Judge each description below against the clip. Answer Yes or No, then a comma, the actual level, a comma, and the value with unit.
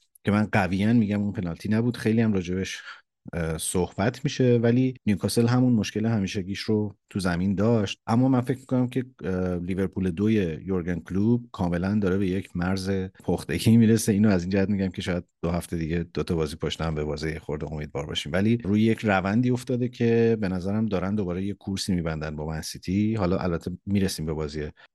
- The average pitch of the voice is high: No, low, 100 Hz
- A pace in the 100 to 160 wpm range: No, fast, 190 wpm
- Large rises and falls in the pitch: No, average, 3.9 semitones